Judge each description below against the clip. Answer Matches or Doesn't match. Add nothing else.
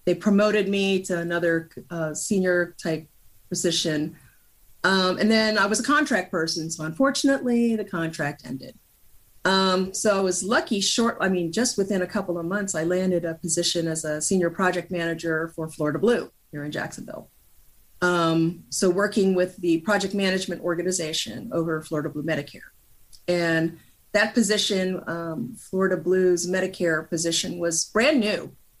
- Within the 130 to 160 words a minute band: Matches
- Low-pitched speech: Doesn't match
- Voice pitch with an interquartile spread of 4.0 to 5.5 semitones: Doesn't match